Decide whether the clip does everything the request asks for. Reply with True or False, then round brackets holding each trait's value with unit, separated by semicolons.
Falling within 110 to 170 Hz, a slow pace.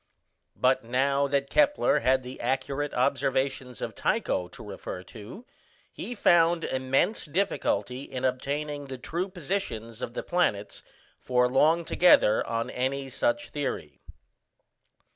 True (135 Hz; 125 wpm)